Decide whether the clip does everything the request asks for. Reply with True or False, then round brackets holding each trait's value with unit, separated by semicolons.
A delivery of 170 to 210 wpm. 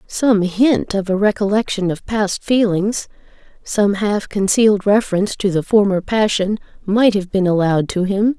False (155 wpm)